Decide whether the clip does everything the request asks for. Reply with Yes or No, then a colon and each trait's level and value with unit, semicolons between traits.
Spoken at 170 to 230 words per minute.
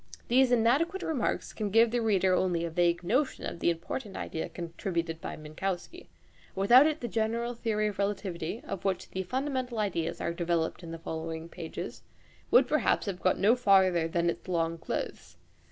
Yes: average, 175 wpm